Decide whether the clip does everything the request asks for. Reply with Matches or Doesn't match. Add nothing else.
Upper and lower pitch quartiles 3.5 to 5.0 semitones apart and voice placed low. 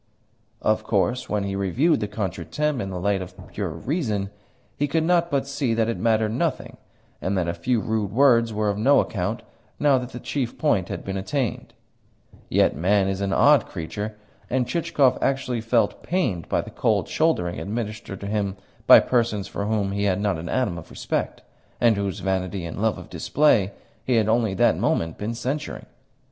Matches